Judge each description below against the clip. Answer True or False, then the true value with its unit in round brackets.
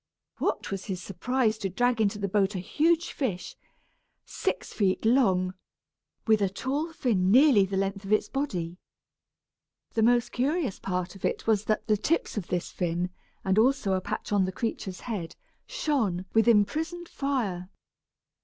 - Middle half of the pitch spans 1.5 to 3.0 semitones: False (5.0 semitones)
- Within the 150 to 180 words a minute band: True (165 wpm)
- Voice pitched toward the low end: False (210 Hz)